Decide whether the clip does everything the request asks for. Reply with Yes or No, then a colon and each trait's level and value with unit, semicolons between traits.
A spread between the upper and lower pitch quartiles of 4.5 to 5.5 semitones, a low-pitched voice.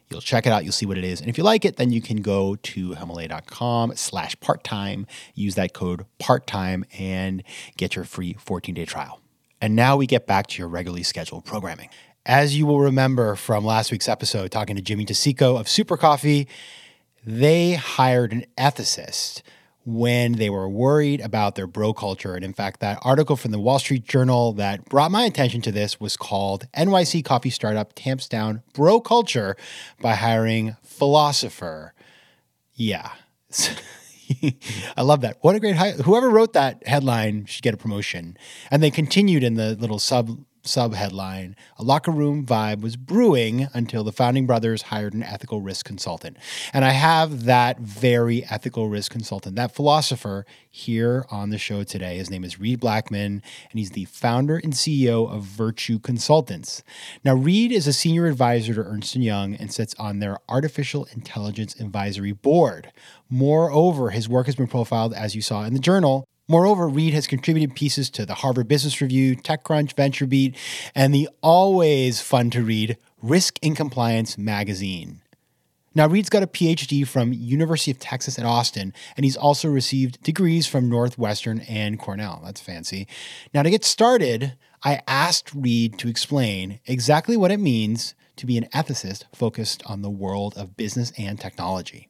Yes: average, 5.1 semitones; low, 120 Hz